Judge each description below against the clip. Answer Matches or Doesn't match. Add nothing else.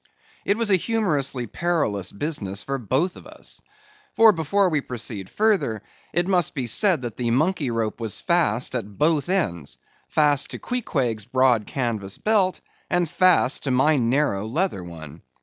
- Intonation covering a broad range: Matches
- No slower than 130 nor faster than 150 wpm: Doesn't match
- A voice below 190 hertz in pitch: Matches